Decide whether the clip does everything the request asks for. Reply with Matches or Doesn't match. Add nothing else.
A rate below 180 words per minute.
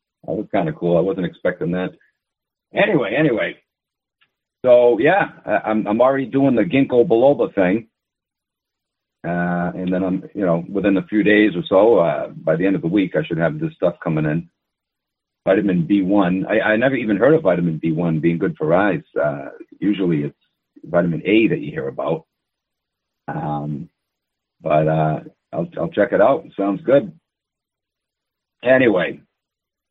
Matches